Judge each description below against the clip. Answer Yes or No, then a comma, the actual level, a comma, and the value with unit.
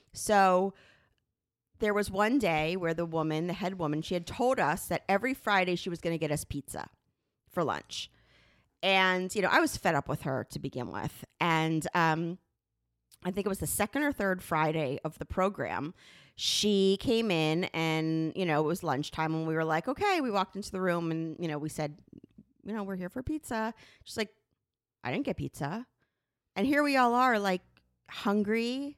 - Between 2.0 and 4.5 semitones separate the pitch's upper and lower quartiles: No, average, 4.9 semitones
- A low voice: No, medium, 180 Hz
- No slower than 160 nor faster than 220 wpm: Yes, average, 195 wpm